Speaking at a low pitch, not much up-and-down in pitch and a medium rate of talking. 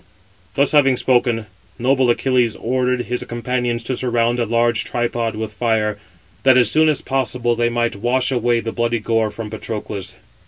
Yes: low, 120 Hz; narrow, 1.8 semitones; average, 165 wpm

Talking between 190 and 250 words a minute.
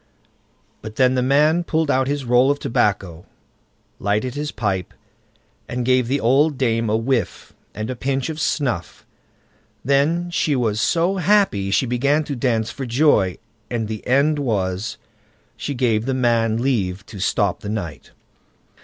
No: average, 155 wpm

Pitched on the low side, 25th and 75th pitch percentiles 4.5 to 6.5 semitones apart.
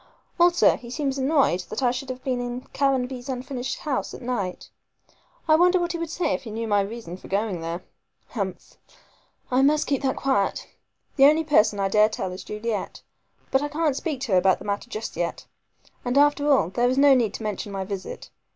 No: very high, 250 Hz; average, 5.3 semitones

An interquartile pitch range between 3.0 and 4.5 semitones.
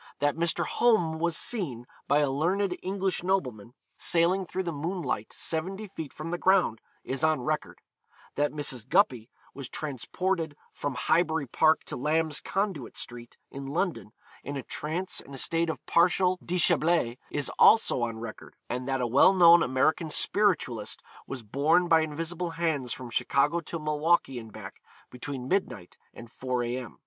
No: average, 5.1 semitones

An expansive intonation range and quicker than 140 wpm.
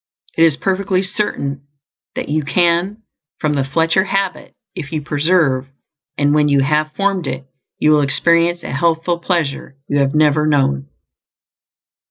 No: average, 3.5 semitones; average, 150 wpm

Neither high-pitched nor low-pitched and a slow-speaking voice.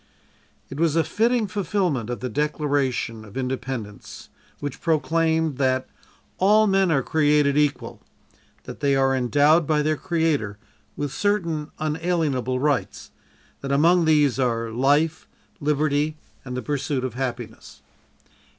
Yes: medium, 145 Hz; slow, 130 wpm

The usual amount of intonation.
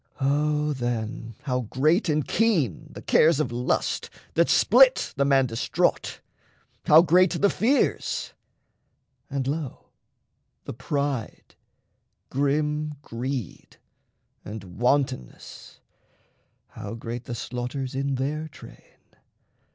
Yes: average, 3.8 semitones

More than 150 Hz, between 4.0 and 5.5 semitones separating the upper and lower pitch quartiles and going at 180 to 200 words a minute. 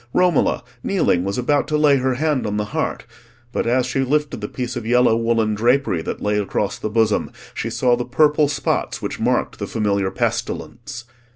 No: low, 120 Hz; average, 4.5 semitones; average, 190 wpm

